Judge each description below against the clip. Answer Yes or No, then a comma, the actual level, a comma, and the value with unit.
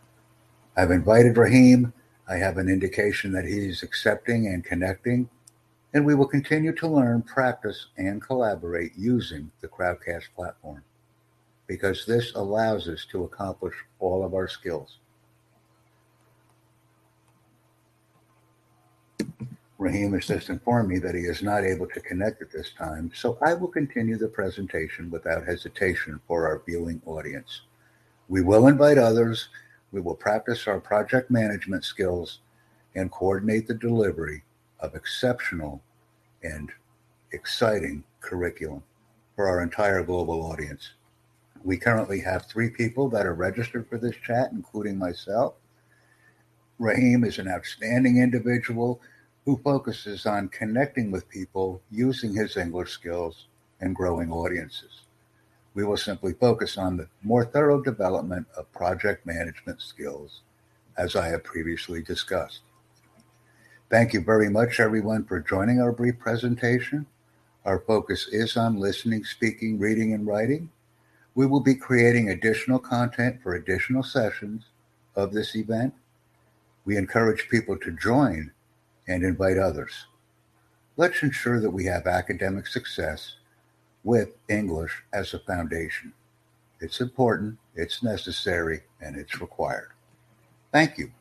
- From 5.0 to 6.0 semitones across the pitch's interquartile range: No, average, 4.0 semitones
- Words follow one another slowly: Yes, slow, 130 wpm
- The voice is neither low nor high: No, low, 110 Hz